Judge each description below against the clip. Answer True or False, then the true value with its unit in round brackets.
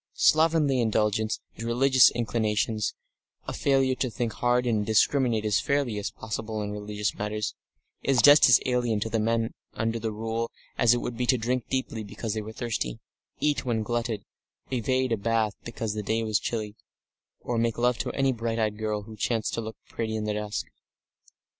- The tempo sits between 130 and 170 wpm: False (185 wpm)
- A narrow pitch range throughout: True (2.3 semitones)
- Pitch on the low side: True (115 Hz)